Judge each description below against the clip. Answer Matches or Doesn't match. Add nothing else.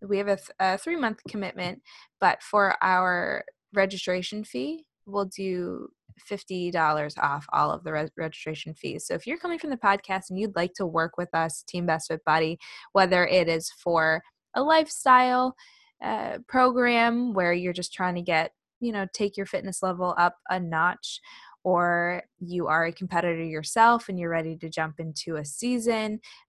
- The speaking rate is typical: Matches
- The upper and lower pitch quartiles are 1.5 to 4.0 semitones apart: Doesn't match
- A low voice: Doesn't match